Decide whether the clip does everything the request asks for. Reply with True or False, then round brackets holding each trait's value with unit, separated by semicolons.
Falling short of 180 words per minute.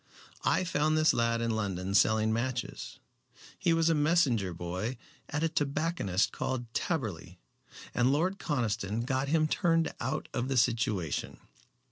True (140 wpm)